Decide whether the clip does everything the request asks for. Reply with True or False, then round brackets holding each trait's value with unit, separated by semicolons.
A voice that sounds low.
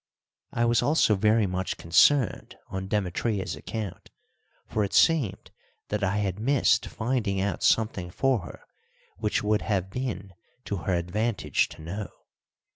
True (105 Hz)